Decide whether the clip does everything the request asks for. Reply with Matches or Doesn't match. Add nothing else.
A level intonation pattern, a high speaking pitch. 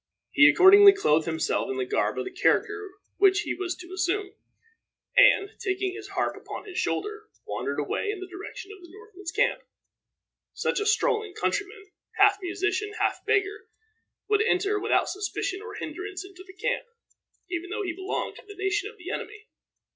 Matches